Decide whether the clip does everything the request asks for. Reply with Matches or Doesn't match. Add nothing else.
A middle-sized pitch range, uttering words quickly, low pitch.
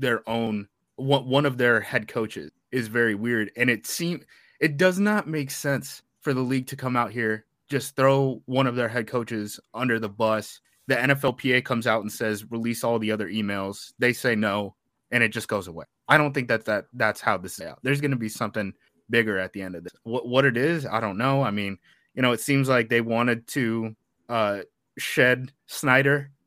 Matches